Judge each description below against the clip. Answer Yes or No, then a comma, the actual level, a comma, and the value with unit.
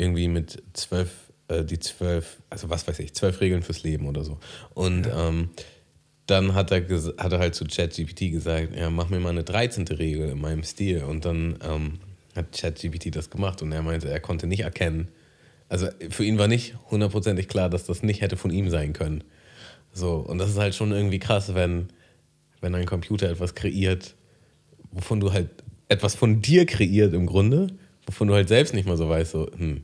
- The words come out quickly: Yes, fast, 200 wpm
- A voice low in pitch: Yes, very low, 90 Hz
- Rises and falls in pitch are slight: No, average, 3.4 semitones